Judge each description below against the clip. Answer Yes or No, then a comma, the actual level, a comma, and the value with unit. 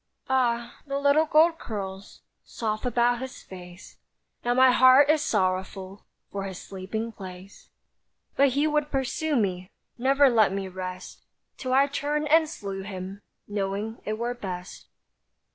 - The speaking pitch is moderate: No, high, 230 Hz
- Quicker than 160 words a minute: No, average, 145 wpm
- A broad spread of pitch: Yes, wide, 6.0 semitones